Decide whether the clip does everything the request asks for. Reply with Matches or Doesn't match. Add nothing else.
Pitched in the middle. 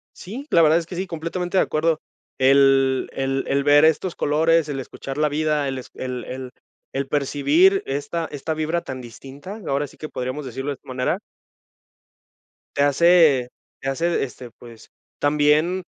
Matches